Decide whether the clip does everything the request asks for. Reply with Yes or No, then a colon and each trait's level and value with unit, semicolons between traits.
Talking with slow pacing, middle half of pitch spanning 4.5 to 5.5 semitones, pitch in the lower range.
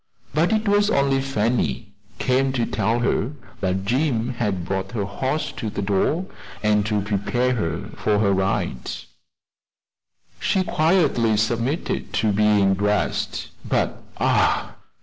Yes: slow, 130 wpm; average, 5.0 semitones; low, 110 Hz